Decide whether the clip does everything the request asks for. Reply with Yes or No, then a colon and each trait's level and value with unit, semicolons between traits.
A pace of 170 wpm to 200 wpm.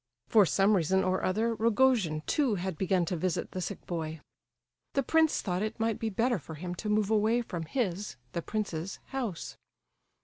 Yes: average, 180 wpm